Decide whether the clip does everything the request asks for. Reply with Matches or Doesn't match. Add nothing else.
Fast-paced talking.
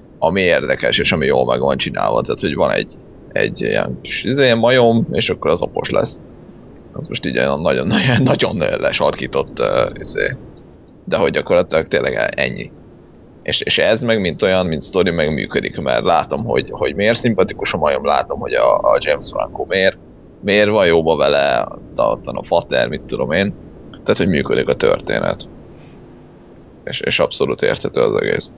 Matches